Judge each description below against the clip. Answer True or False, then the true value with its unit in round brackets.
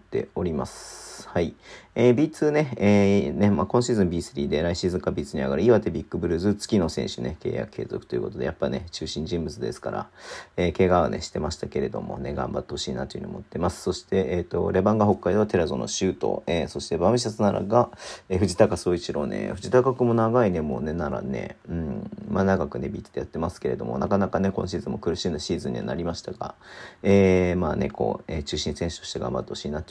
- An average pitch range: True (3.4 semitones)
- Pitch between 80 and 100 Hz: True (95 Hz)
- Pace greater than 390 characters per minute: True (425 characters per minute)